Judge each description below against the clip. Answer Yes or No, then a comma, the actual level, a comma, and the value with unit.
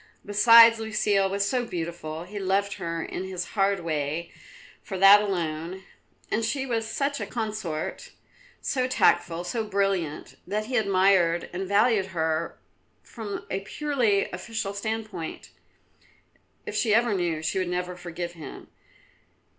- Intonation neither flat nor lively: Yes, average, 4.0 semitones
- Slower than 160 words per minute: Yes, average, 140 wpm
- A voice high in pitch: Yes, high, 195 Hz